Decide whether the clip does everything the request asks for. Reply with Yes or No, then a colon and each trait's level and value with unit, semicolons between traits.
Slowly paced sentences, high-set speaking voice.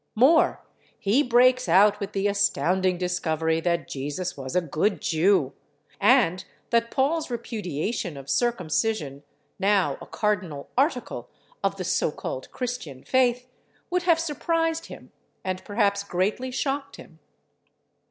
Yes: slow, 130 wpm; high, 205 Hz